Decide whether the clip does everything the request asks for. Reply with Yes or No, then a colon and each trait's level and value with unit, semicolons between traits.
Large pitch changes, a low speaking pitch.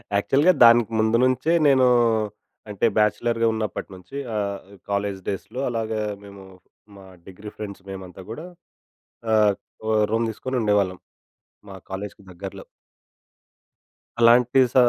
No: average, 2.8 semitones; low, 105 Hz